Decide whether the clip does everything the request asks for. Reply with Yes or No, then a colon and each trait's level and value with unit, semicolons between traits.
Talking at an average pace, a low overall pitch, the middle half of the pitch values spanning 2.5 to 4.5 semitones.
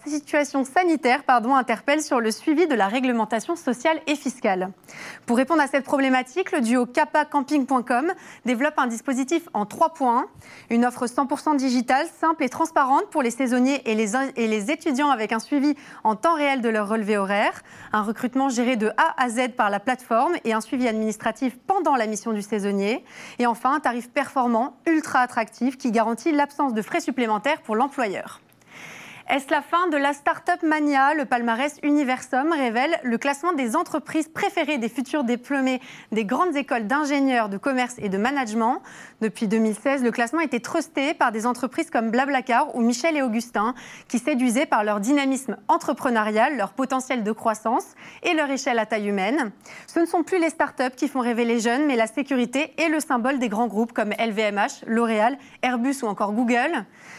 No: average, 180 wpm; very high, 260 Hz; average, 4.2 semitones